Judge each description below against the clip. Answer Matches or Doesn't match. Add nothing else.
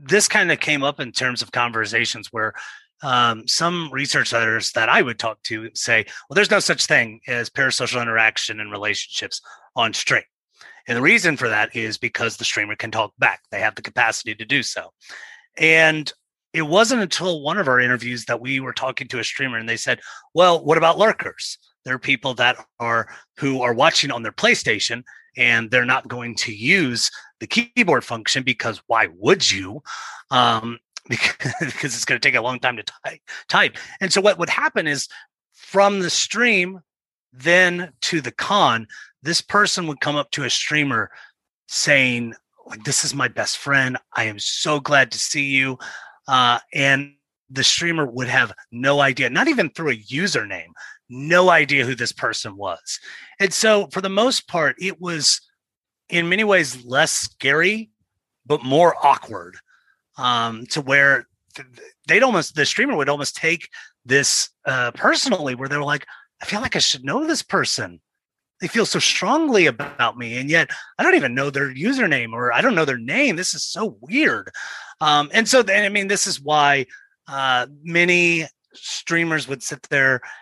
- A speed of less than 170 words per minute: Doesn't match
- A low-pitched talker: Doesn't match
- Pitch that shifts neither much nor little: Doesn't match